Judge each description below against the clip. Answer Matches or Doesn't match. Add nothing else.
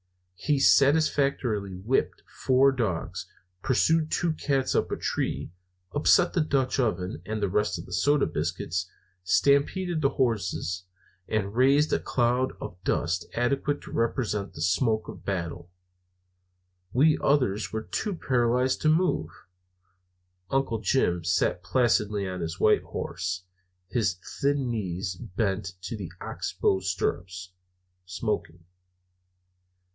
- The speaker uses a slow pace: Matches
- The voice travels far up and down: Matches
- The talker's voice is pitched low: Matches